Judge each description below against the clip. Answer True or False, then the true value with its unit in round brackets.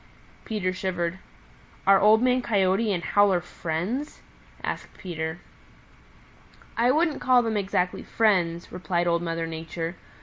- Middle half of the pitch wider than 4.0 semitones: True (4.4 semitones)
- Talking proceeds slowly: True (125 wpm)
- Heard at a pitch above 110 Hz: True (185 Hz)